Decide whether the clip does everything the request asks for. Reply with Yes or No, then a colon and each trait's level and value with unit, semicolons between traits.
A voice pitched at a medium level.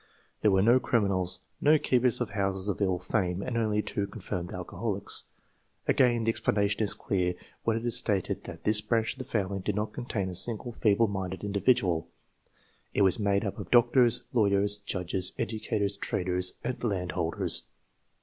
No: low, 100 Hz